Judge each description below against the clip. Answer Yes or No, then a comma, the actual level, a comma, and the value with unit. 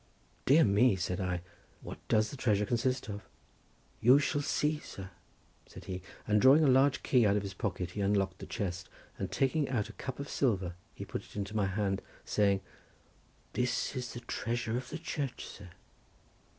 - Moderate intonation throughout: Yes, average, 4.9 semitones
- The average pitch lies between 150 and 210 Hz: No, low, 110 Hz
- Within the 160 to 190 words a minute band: Yes, average, 180 wpm